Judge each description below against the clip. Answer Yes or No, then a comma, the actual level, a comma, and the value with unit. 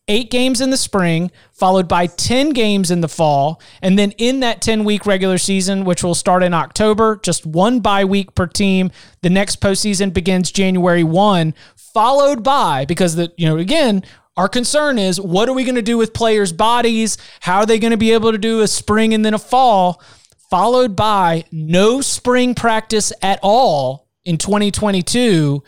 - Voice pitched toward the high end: Yes, high, 200 Hz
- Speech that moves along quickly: No, average, 185 wpm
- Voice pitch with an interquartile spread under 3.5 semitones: No, average, 4.1 semitones